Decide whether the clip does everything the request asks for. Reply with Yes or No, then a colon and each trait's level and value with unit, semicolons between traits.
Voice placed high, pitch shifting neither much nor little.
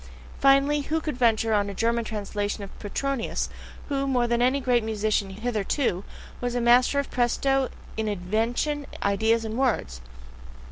Yes: high, 235 Hz; average, 4.0 semitones